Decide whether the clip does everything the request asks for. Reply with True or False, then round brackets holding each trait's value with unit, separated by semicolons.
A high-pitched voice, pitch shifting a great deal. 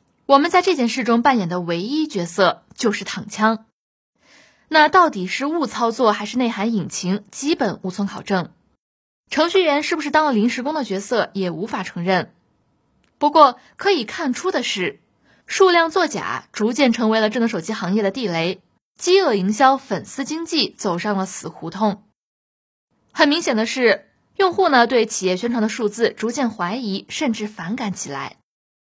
True (225 Hz; 6.4 semitones)